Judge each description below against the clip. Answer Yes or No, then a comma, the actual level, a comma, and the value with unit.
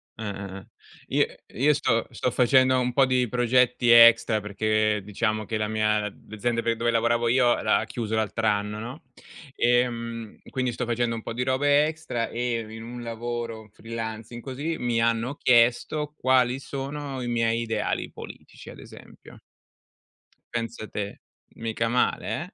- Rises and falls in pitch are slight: Yes, narrow, 2.0 semitones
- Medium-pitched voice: No, low, 115 Hz